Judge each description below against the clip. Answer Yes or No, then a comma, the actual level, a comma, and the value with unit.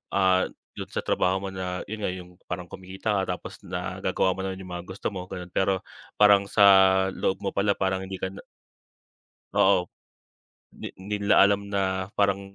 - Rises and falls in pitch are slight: Yes, narrow, 1.1 semitones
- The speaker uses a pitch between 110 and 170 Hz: No, very low, 95 Hz